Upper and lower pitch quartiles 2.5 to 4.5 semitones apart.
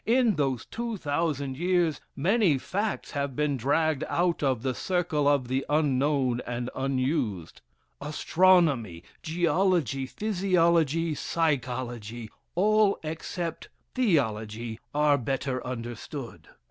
No: average, 5.1 semitones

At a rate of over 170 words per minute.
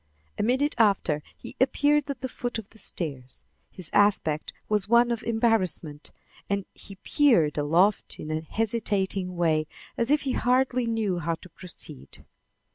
No: average, 155 wpm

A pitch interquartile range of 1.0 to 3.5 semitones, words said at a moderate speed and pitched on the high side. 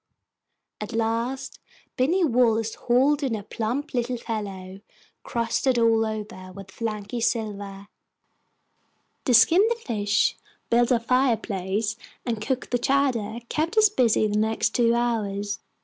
No: average, 3.1 semitones; slow, 130 wpm; high, 230 Hz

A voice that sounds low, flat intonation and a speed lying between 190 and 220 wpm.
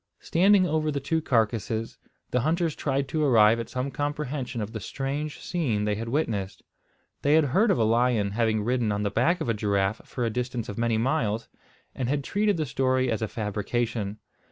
No: low, 125 Hz; average, 4.9 semitones; average, 200 wpm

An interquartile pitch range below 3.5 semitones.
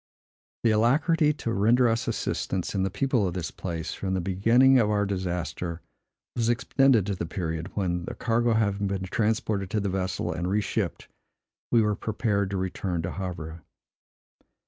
No: average, 3.9 semitones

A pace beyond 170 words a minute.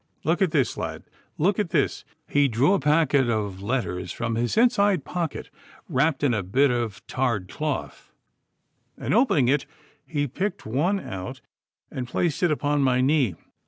No: average, 160 wpm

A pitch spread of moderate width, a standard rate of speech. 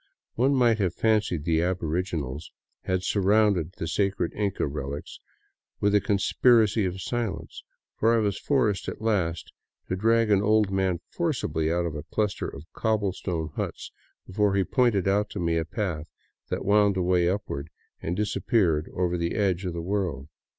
Yes: average, 3.9 semitones; average, 165 wpm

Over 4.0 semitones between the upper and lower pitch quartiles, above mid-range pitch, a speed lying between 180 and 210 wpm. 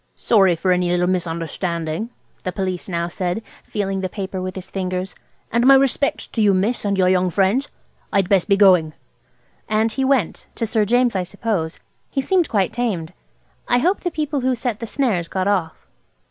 Yes: average, 4.6 semitones; high, 195 Hz; average, 185 wpm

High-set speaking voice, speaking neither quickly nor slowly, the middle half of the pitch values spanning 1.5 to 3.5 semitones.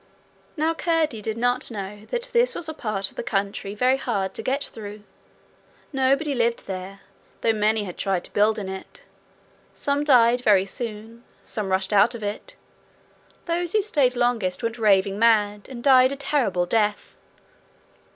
No: high, 225 Hz; average, 165 wpm; average, 4.6 semitones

